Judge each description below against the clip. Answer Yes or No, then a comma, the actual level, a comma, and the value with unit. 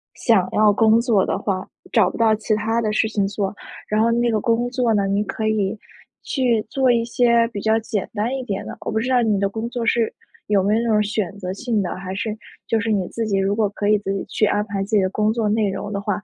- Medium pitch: No, high, 215 Hz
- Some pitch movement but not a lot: No, narrow, 2.3 semitones